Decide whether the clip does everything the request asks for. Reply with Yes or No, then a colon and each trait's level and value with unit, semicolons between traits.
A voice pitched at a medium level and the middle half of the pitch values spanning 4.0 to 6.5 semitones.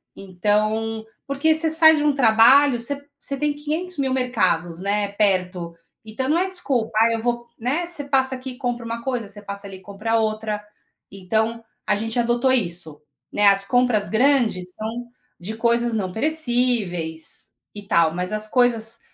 No: high, 225 Hz; average, 4.5 semitones